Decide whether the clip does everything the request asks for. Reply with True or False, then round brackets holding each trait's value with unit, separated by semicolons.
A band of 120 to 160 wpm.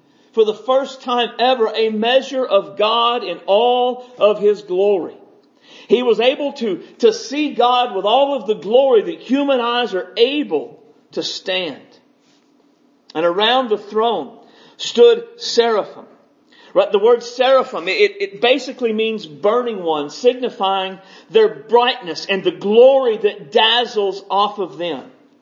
True (140 wpm)